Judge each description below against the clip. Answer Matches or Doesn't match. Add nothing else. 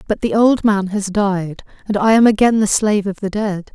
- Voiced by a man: Doesn't match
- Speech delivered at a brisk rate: Matches